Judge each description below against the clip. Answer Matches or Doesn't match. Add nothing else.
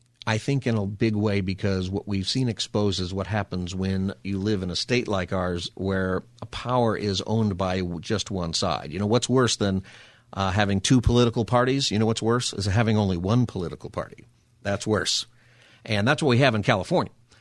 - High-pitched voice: Doesn't match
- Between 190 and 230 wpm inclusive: Matches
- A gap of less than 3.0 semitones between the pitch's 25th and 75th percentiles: Doesn't match